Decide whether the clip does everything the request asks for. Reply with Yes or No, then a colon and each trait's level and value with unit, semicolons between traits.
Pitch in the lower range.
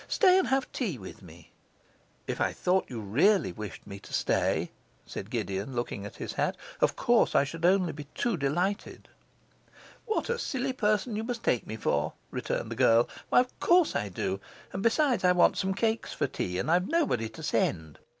No: medium, 180 Hz